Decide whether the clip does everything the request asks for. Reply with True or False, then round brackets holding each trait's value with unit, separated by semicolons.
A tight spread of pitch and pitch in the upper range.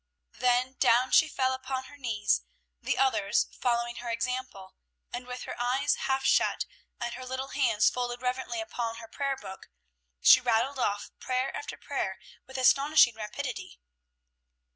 True (2.0 semitones; 250 Hz)